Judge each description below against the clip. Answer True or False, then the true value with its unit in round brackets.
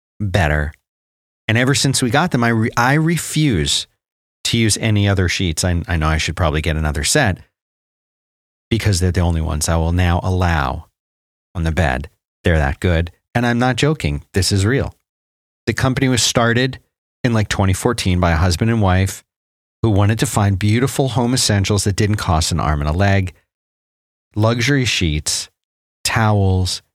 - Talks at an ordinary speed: True (175 wpm)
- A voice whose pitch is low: True (95 Hz)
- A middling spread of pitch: False (5.9 semitones)